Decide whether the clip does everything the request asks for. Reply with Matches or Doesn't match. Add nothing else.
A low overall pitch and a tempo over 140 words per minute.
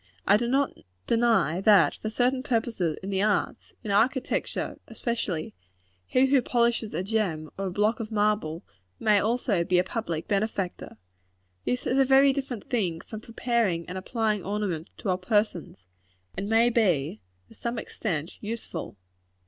Doesn't match